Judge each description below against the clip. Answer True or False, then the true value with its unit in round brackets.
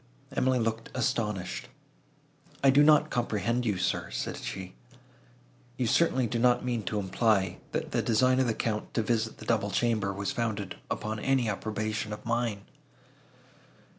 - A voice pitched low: True (115 Hz)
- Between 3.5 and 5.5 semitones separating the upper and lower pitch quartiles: False (2.7 semitones)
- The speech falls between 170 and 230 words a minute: False (155 wpm)